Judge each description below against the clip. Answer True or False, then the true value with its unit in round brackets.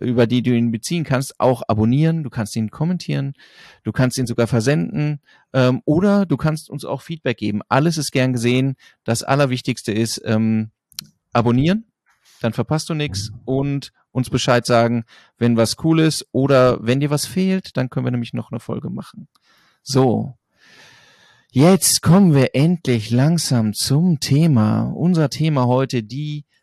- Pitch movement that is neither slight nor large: True (4.1 semitones)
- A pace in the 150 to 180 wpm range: True (160 wpm)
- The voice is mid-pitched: False (130 Hz)